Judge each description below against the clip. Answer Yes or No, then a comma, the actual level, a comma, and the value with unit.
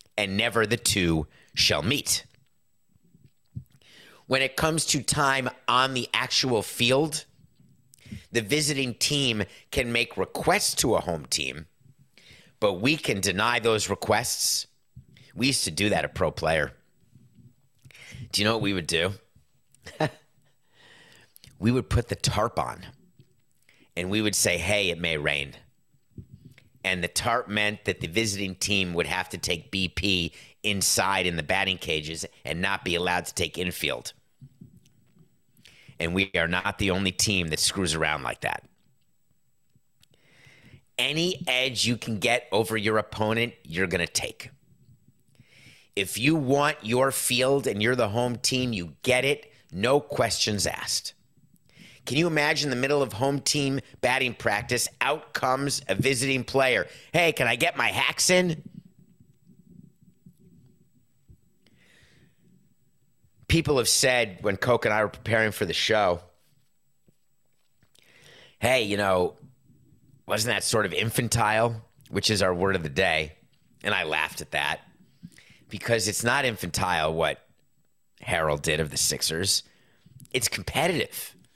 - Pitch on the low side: Yes, low, 115 Hz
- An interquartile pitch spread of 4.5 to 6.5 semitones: Yes, wide, 5.5 semitones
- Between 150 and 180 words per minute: No, average, 140 wpm